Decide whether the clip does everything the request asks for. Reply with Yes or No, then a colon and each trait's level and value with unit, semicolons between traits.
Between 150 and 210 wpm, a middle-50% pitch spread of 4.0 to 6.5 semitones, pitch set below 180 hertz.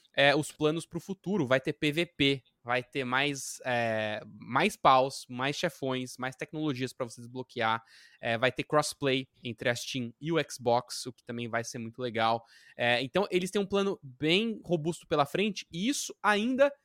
Yes: fast, 185 wpm; wide, 5.5 semitones; medium, 140 Hz